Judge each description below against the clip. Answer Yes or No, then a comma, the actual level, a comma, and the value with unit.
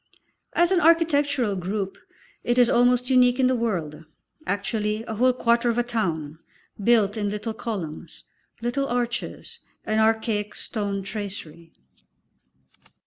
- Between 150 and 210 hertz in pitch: No, high, 225 Hz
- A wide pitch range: No, average, 3.5 semitones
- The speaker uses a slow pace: Yes, slow, 130 wpm